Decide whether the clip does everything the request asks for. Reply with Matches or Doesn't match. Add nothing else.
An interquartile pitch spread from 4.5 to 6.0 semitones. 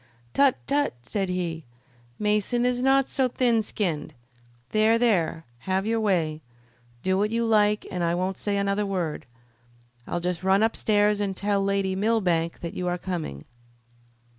Doesn't match